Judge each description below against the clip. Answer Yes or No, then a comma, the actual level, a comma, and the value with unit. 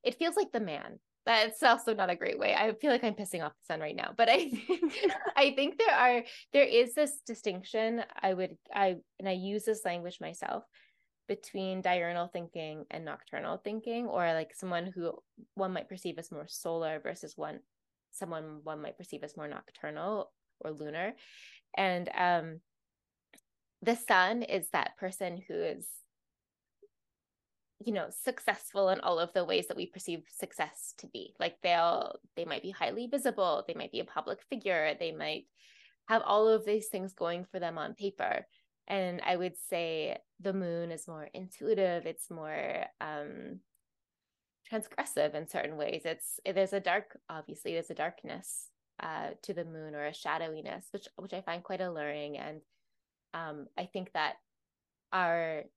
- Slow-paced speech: No, average, 170 wpm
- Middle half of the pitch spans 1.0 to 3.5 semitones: No, average, 5.0 semitones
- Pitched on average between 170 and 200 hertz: Yes, medium, 185 Hz